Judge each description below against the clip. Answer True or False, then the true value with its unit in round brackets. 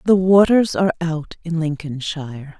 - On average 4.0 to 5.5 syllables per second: True (4.8 syllables/s)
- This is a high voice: False (165 Hz)